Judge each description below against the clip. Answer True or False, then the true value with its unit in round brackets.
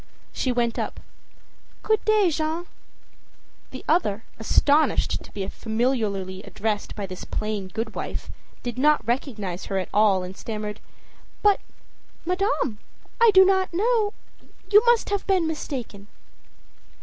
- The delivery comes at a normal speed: False (125 wpm)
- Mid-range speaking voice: False (245 Hz)